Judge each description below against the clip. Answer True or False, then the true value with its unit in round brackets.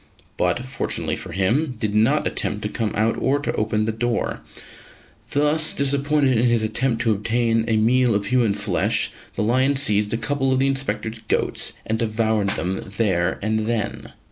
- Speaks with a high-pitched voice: False (115 Hz)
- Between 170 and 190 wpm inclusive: True (175 wpm)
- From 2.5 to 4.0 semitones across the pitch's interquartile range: True (3.3 semitones)